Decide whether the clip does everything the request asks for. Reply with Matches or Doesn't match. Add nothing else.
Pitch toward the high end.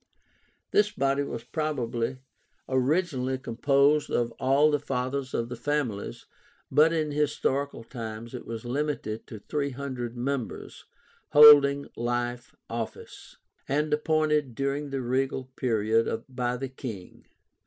Doesn't match